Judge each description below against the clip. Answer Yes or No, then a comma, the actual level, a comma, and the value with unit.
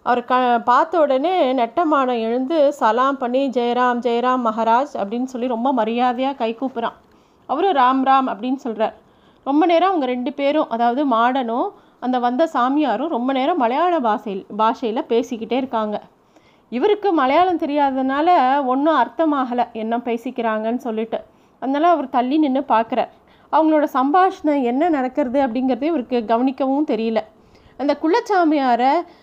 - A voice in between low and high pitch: No, very high, 260 Hz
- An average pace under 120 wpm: No, average, 125 wpm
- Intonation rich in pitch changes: No, average, 4.0 semitones